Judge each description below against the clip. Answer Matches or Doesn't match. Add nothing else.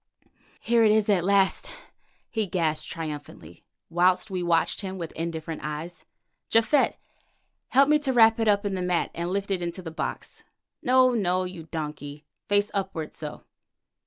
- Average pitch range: Matches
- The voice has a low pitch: Doesn't match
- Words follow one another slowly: Doesn't match